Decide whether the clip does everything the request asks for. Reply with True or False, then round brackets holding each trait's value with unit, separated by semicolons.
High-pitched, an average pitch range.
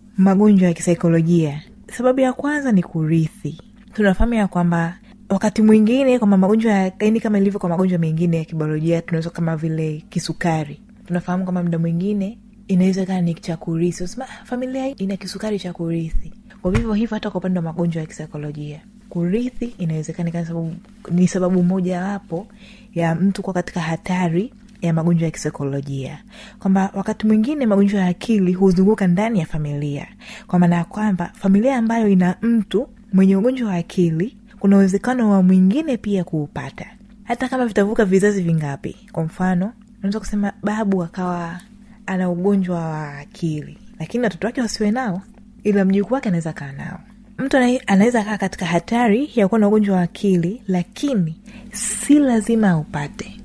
True (195 Hz; 4.0 semitones)